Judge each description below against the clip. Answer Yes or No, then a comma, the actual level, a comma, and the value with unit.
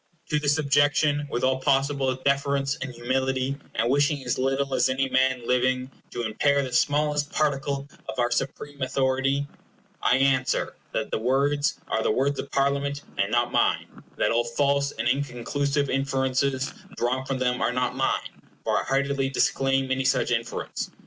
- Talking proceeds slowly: No, average, 170 wpm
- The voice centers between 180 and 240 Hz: No, low, 135 Hz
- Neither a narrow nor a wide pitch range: No, narrow, 1.6 semitones